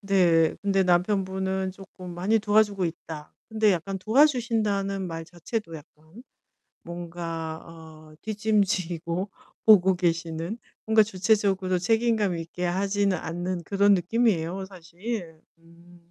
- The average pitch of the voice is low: No, medium, 185 Hz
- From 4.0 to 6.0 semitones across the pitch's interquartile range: No, average, 3.3 semitones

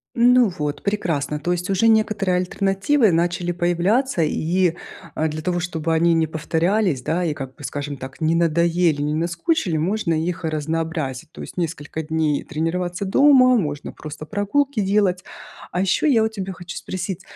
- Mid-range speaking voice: Yes, medium, 175 Hz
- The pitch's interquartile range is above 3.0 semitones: Yes, average, 3.7 semitones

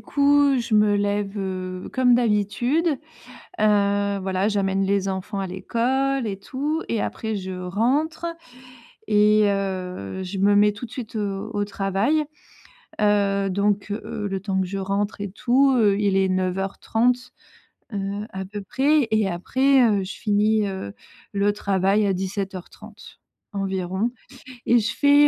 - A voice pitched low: No, high, 205 Hz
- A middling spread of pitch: Yes, average, 3.0 semitones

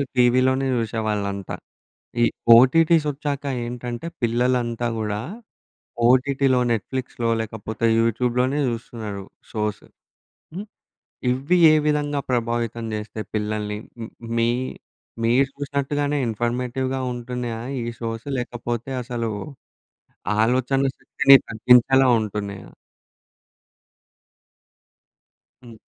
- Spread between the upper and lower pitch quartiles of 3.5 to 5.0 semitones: No, average, 2.8 semitones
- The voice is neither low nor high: No, low, 120 Hz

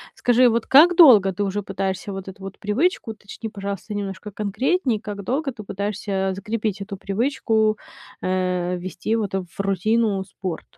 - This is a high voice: Yes, high, 205 Hz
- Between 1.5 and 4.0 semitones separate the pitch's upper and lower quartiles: Yes, narrow, 2.5 semitones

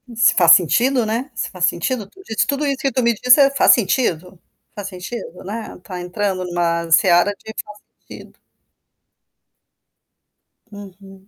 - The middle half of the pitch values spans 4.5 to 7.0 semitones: Yes, average, 5.0 semitones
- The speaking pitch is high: Yes, high, 205 Hz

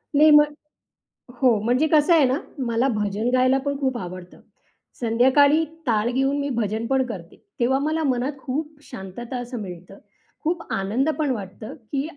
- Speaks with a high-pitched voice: Yes, very high, 255 Hz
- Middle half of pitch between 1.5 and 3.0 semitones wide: No, average, 4.3 semitones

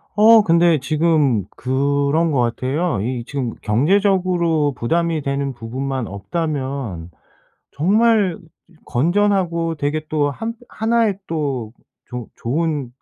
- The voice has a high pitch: No, medium, 150 Hz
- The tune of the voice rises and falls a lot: No, average, 4.6 semitones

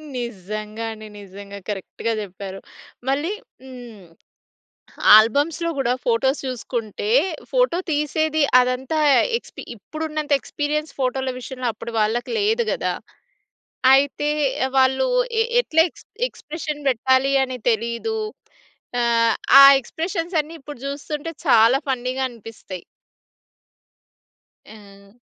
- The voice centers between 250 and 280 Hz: Yes, very high, 260 Hz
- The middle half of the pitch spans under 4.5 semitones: No, average, 5.1 semitones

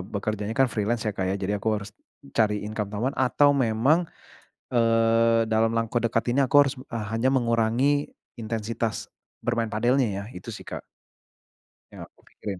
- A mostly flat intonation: Yes, narrow, 2.3 semitones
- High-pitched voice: No, low, 115 Hz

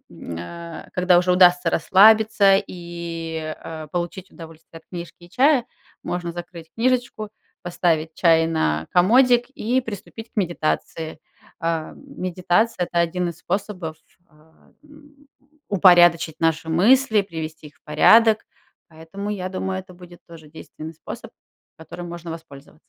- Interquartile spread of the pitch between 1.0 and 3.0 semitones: No, average, 3.8 semitones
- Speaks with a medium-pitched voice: Yes, medium, 175 Hz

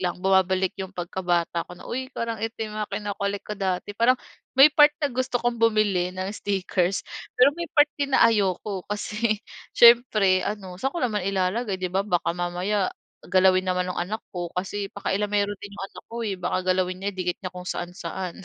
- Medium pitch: No, high, 195 Hz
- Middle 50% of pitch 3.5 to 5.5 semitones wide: No, average, 2.9 semitones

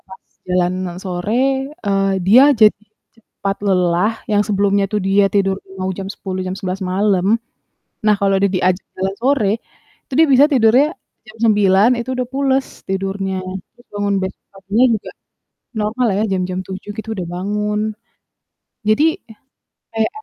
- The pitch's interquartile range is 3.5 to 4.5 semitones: No, average, 2.7 semitones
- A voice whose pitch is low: No, high, 200 Hz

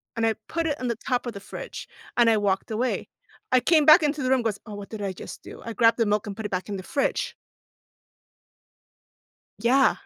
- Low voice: No, high, 230 Hz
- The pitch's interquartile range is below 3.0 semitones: No, average, 3.9 semitones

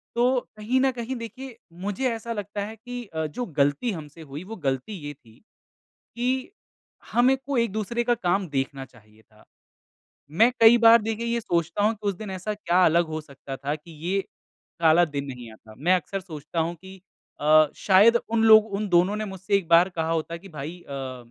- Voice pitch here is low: No, high, 190 Hz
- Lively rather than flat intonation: Yes, wide, 6.4 semitones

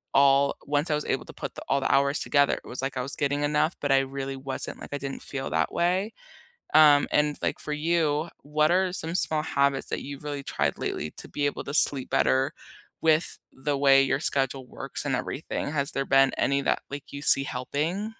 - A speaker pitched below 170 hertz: Yes, medium, 140 Hz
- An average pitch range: No, narrow, 1.8 semitones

